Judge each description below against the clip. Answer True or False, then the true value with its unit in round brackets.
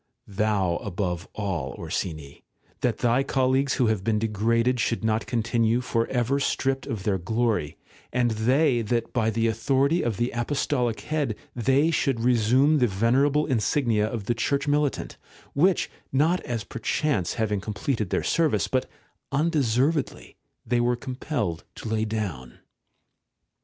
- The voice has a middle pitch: False (120 Hz)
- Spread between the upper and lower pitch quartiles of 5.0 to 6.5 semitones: False (3.8 semitones)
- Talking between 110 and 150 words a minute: True (145 wpm)